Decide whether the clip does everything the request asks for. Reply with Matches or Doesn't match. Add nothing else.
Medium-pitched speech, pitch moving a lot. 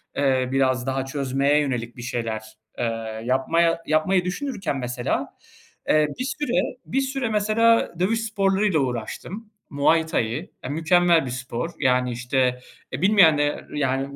Matches